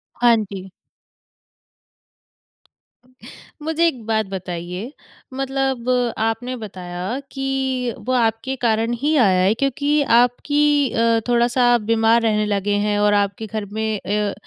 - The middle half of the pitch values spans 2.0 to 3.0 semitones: No, average, 3.8 semitones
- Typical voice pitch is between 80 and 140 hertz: No, high, 230 Hz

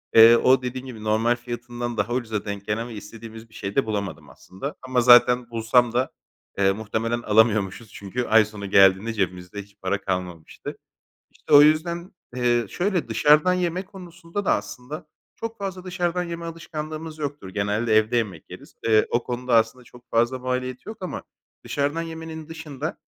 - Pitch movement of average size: No, wide, 6.0 semitones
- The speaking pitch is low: Yes, low, 120 Hz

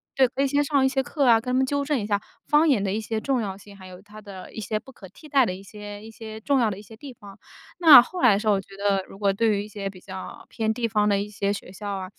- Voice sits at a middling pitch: No, high, 215 Hz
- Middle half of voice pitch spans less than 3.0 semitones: No, average, 4.4 semitones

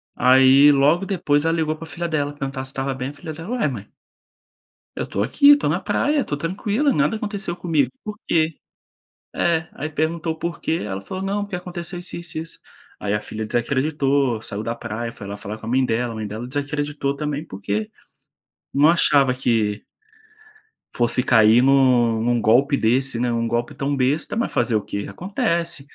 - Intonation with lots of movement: Yes, wide, 5.8 semitones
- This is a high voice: No, medium, 140 Hz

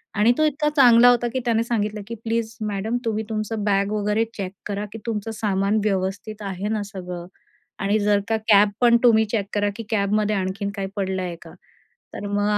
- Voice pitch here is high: Yes, high, 210 Hz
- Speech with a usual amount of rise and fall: No, narrow, 2.0 semitones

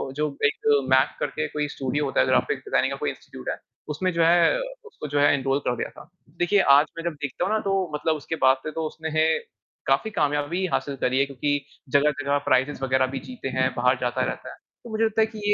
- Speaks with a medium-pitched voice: Yes, medium, 145 Hz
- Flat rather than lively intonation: No, average, 4.3 semitones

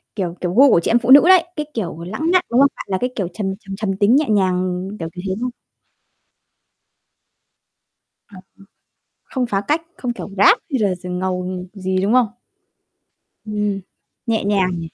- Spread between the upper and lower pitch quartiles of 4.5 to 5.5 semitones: Yes, average, 4.9 semitones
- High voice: Yes, high, 205 Hz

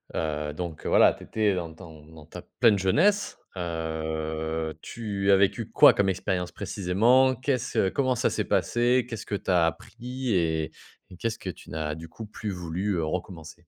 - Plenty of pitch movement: Yes, wide, 5.7 semitones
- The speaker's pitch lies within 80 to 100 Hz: Yes, very low, 90 Hz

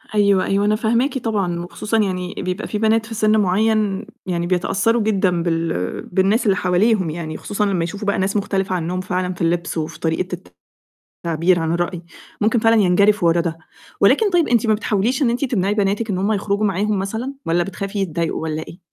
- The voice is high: Yes, high, 195 Hz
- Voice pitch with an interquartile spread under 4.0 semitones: Yes, average, 3.5 semitones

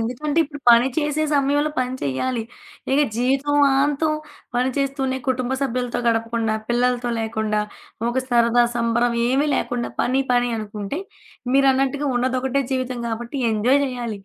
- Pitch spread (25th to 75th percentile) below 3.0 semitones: Yes, narrow, 2.6 semitones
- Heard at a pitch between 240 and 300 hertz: Yes, very high, 250 Hz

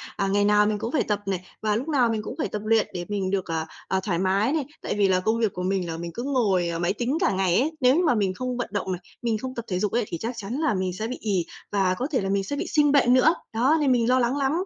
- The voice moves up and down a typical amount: Yes, average, 4.9 semitones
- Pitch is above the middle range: Yes, high, 215 Hz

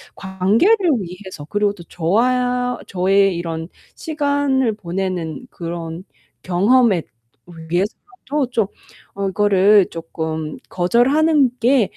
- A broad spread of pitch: Yes, wide, 6.1 semitones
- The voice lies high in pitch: Yes, high, 200 Hz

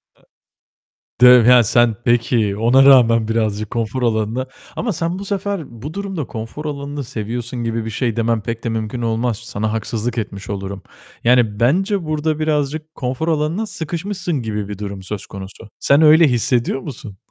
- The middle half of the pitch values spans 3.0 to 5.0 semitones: No, wide, 5.4 semitones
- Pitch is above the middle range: No, low, 120 Hz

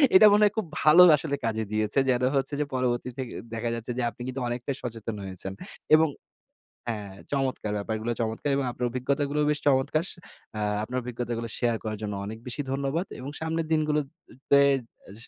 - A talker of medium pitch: No, low, 125 Hz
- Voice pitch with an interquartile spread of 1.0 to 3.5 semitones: No, average, 4.2 semitones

